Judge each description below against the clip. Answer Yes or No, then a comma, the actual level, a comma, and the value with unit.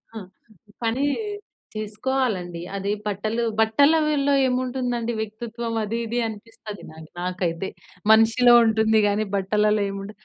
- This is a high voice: Yes, high, 220 Hz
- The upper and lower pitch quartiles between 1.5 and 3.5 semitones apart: Yes, average, 2.9 semitones